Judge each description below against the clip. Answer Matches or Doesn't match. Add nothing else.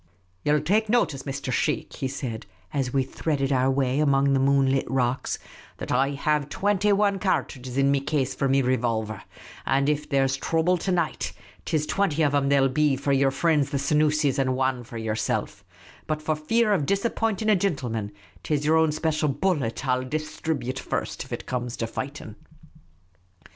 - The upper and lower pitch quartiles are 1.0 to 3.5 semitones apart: Matches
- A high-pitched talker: Doesn't match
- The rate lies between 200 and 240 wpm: Matches